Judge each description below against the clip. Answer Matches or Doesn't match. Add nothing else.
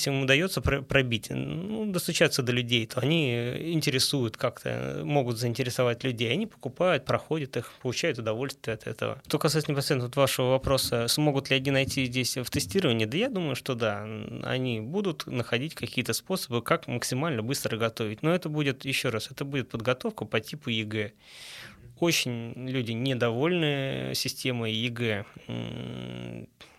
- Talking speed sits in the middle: Matches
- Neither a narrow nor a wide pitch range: Matches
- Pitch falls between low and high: Doesn't match